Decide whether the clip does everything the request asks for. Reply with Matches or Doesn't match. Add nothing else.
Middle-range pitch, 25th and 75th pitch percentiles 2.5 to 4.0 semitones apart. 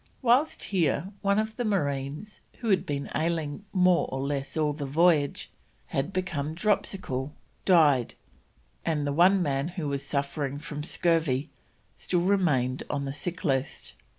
Doesn't match